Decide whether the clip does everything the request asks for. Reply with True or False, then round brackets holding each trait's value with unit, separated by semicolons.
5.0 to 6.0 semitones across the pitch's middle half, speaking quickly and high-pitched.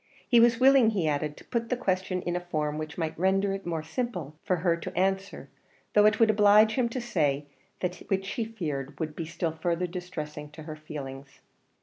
False (5.3 semitones; 210 wpm; 180 Hz)